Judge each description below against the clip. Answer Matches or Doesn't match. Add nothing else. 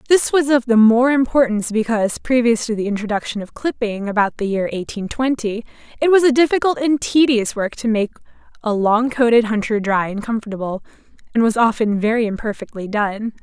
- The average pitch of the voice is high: Matches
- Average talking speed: Matches